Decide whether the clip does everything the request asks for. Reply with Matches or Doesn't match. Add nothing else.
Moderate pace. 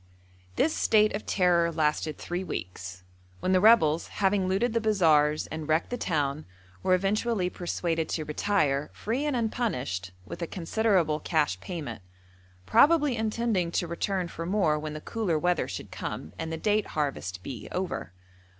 Matches